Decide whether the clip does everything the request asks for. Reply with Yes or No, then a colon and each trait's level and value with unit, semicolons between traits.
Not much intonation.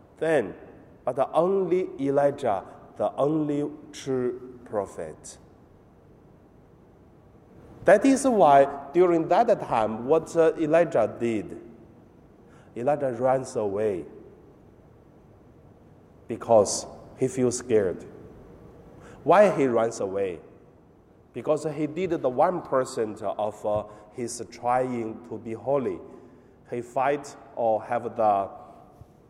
No: average, 5.1 semitones